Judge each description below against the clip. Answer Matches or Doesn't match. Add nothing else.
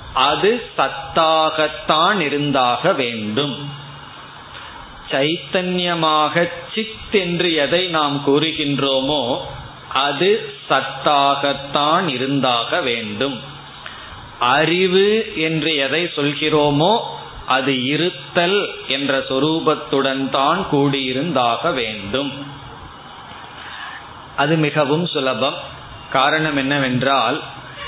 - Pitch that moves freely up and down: Doesn't match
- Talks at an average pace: Doesn't match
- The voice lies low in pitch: Doesn't match